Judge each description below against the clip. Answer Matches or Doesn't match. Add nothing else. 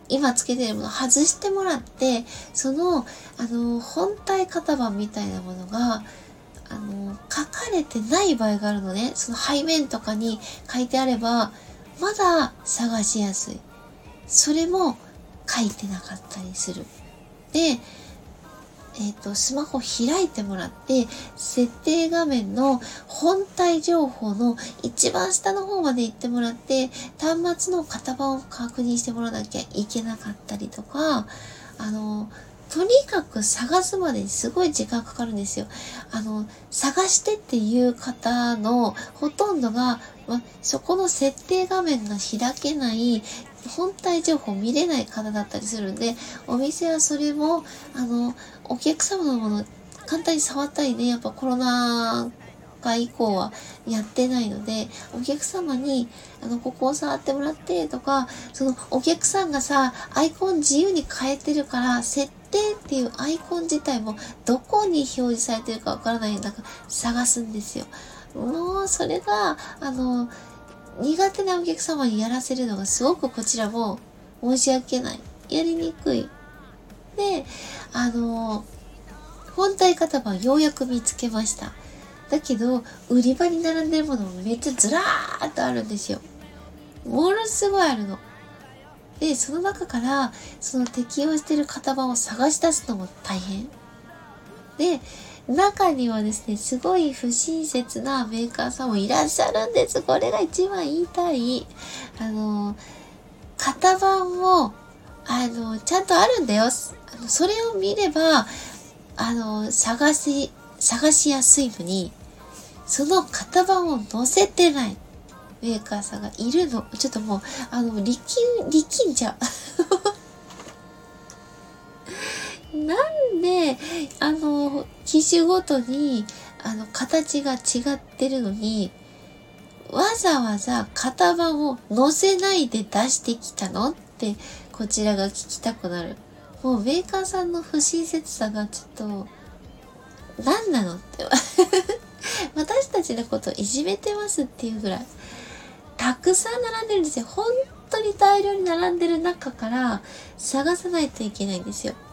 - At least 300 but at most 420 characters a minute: Doesn't match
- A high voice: Matches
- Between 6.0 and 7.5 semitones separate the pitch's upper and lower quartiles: Matches